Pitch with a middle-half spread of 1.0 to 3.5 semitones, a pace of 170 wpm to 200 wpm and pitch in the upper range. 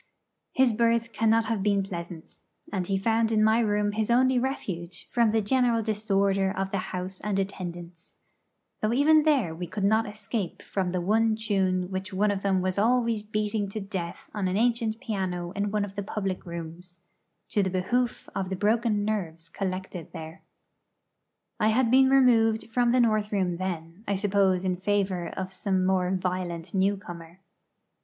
Yes: average, 3.2 semitones; average, 175 wpm; high, 200 Hz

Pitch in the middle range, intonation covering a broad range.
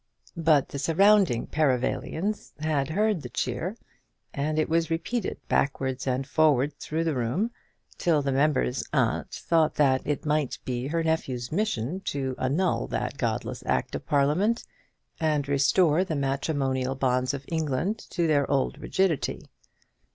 No: medium, 150 Hz; average, 3.7 semitones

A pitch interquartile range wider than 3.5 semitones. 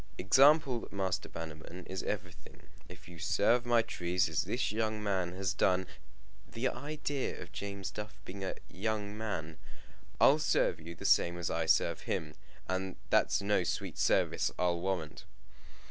Yes: average, 4.1 semitones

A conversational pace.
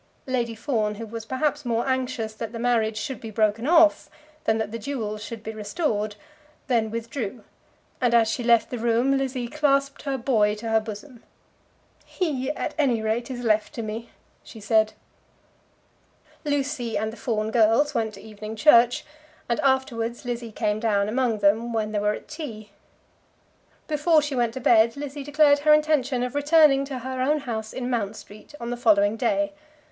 Yes: average, 180 wpm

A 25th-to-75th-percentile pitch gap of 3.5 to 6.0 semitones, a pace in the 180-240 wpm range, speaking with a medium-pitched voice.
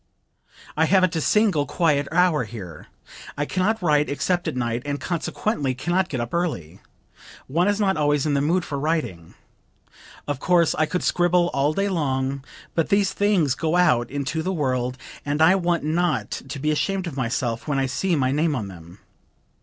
Yes: average, 4.9 semitones; average, 190 wpm; medium, 155 Hz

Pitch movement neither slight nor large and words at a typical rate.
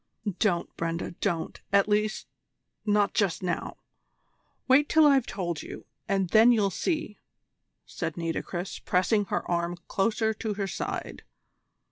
No: average, 4.0 semitones; slow, 130 wpm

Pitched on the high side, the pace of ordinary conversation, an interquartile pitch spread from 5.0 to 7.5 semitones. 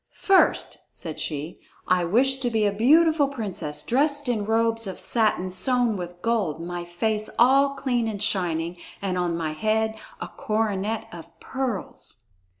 Yes: high, 215 Hz; average, 150 wpm; wide, 5.5 semitones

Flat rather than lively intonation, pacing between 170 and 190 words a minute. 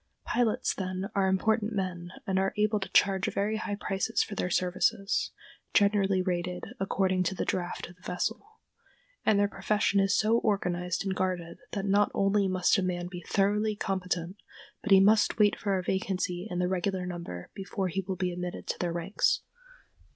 Yes: narrow, 2.1 semitones; average, 185 wpm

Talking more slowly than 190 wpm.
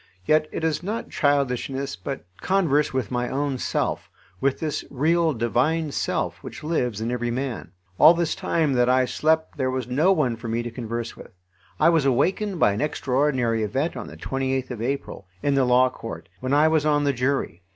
No: average, 195 wpm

